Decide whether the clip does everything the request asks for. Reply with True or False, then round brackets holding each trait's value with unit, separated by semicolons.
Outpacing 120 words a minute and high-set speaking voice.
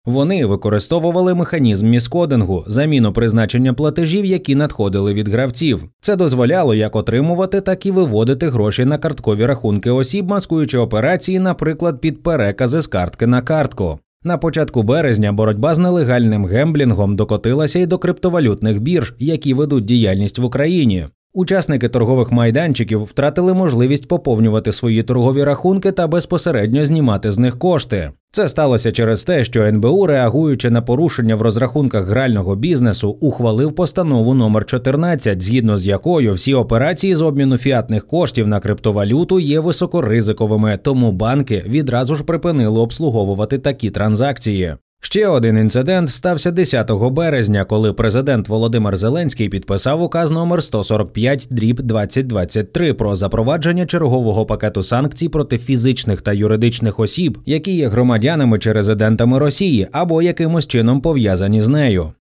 False (135 wpm; 125 Hz)